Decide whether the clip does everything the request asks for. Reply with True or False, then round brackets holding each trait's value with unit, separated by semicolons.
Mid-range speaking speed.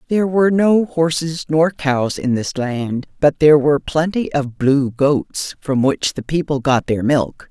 True (185 wpm)